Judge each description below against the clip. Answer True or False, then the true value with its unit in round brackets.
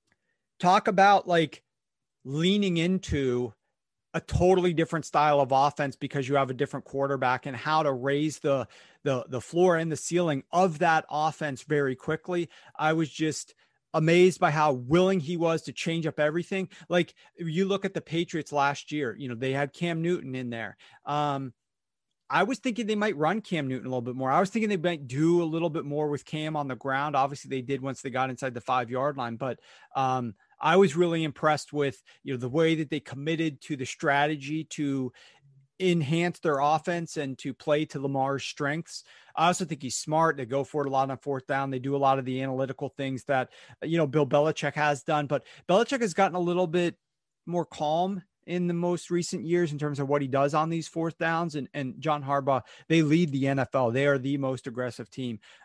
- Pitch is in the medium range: True (150 Hz)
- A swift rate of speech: True (210 wpm)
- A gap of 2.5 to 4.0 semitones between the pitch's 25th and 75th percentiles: True (3.7 semitones)